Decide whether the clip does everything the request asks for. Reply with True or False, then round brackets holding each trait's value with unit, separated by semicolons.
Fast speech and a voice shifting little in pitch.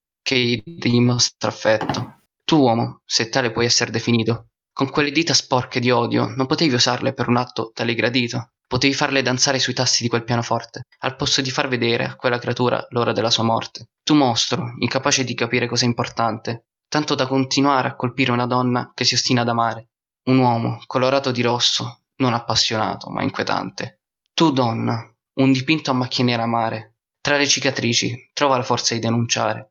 True (180 wpm; 2.2 semitones)